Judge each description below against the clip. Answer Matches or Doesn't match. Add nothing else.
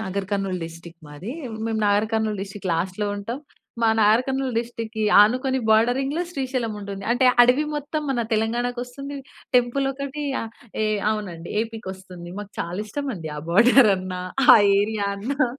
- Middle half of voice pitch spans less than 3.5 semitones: Doesn't match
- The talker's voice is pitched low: Doesn't match